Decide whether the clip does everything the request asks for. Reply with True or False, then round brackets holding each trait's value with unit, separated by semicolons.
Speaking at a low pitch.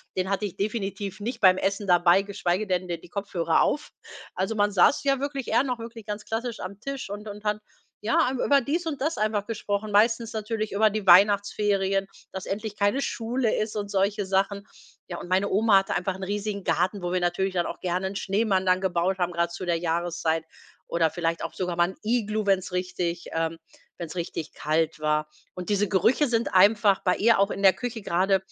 False (195 Hz)